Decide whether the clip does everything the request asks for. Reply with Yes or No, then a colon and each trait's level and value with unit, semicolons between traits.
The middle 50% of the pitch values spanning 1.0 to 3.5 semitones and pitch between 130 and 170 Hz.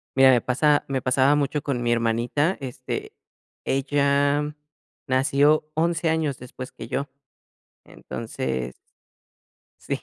Yes: average, 2.7 semitones; medium, 140 Hz